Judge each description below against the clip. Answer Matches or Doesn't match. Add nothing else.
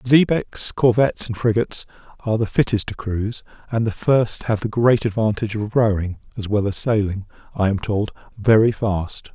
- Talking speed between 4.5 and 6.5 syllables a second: Matches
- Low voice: Matches